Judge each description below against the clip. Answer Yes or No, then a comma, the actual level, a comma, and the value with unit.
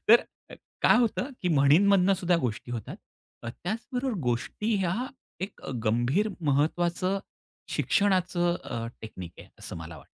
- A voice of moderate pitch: Yes, medium, 175 Hz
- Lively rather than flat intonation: Yes, wide, 8.5 semitones